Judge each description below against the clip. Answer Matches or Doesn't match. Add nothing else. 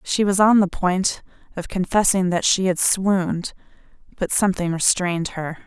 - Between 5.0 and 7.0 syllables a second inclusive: Doesn't match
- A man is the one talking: Doesn't match